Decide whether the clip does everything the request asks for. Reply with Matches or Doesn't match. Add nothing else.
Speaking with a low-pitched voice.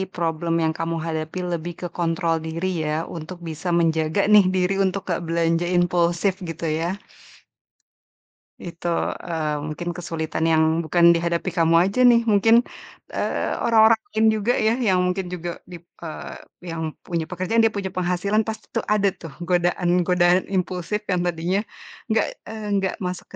Doesn't match